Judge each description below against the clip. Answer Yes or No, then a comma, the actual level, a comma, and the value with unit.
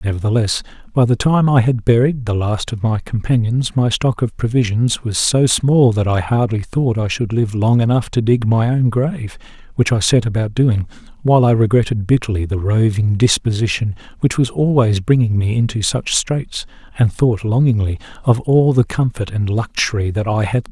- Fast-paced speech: No, average, 190 wpm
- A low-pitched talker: Yes, low, 115 Hz